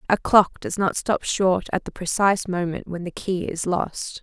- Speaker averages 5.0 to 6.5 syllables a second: No, 4.5 syllables/s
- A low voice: No, medium, 185 Hz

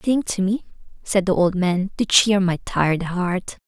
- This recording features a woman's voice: Yes, female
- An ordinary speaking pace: Yes, average, 195 wpm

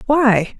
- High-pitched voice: Yes, high, 240 Hz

